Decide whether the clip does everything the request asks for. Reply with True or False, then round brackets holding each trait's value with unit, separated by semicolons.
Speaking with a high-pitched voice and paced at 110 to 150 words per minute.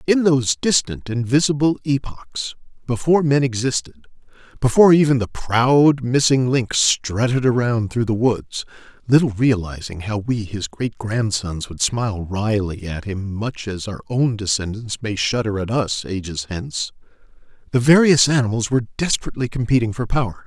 False (120 Hz; 145 wpm)